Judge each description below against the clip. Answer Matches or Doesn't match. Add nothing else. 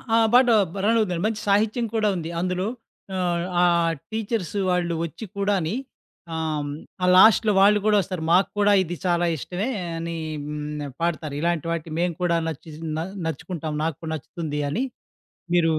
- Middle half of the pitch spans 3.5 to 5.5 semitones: Matches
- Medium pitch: Matches